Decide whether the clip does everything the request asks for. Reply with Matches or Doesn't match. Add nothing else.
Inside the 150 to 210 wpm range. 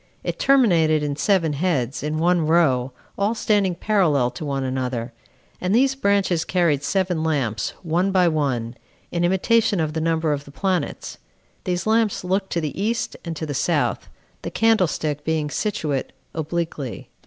Matches